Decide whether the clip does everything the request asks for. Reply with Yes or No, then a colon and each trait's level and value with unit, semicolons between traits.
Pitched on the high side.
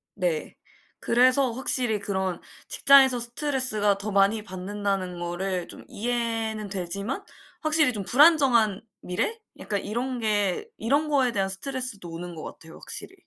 Yes: high, 215 Hz